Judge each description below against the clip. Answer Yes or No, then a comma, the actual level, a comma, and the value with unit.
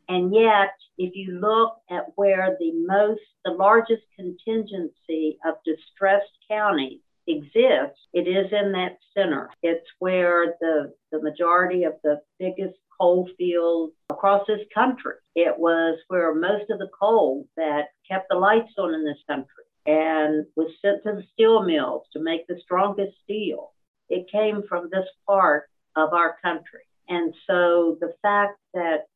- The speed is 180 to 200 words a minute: No, average, 150 wpm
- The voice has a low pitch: No, medium, 180 Hz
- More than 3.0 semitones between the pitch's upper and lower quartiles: Yes, average, 3.6 semitones